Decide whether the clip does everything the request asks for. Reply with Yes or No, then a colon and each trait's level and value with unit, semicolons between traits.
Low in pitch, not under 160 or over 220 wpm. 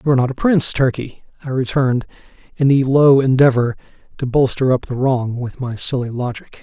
Yes: low, 130 Hz; average, 190 wpm